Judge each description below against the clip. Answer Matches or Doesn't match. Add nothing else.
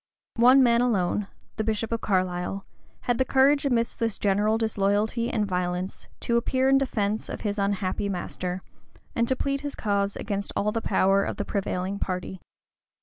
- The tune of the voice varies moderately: Matches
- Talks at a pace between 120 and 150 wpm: Doesn't match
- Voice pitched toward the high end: Matches